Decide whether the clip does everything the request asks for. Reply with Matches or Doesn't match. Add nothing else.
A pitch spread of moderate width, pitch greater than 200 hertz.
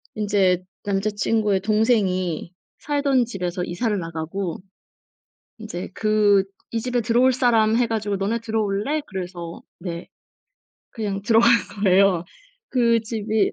Matches